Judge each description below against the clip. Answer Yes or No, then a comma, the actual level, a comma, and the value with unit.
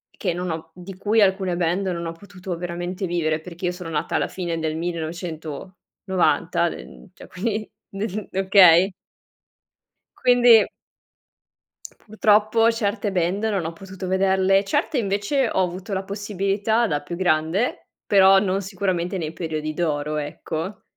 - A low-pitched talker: No, medium, 185 Hz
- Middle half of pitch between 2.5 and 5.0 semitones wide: Yes, average, 2.9 semitones